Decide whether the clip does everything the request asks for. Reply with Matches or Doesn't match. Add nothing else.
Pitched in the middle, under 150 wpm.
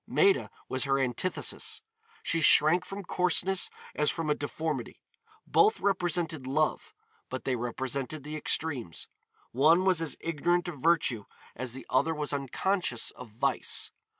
Matches